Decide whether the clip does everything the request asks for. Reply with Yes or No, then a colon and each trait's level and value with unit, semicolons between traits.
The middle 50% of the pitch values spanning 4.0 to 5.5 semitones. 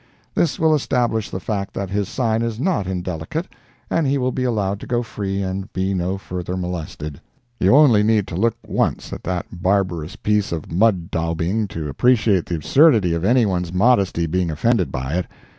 Yes: average, 4.5 semitones